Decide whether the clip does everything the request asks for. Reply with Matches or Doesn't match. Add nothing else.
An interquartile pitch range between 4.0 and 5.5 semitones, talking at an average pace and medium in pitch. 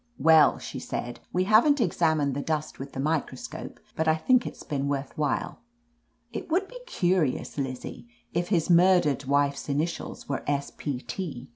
Matches